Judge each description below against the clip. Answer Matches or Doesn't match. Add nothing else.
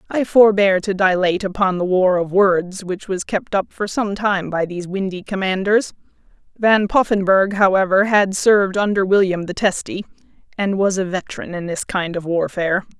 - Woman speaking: Matches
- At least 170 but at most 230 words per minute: Matches